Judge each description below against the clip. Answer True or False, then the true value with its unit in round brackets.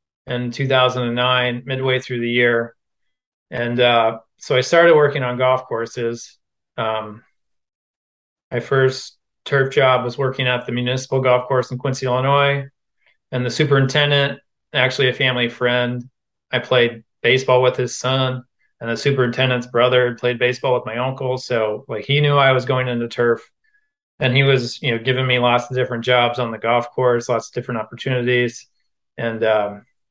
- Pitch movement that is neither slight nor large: False (1.6 semitones)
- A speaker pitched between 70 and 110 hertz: False (125 Hz)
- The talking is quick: False (165 wpm)